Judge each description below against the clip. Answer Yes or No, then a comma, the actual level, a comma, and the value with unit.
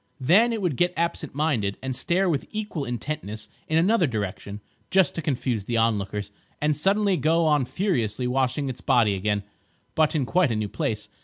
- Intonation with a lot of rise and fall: Yes, wide, 7.5 semitones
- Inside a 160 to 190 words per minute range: Yes, average, 180 wpm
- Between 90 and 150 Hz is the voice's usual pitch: Yes, medium, 140 Hz